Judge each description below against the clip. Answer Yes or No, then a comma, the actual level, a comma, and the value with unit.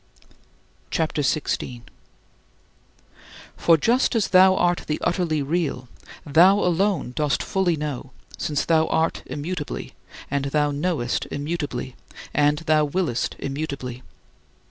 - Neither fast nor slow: No, slow, 115 wpm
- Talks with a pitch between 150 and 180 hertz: Yes, medium, 155 Hz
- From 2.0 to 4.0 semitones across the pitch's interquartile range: Yes, average, 3.6 semitones